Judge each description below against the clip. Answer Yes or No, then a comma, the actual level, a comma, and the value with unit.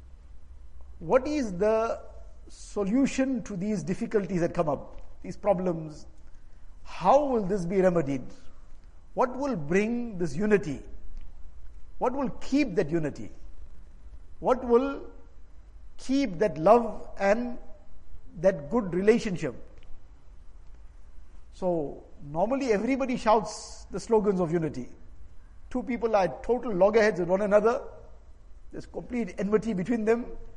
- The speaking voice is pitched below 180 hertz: No, medium, 185 Hz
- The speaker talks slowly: Yes, slow, 110 wpm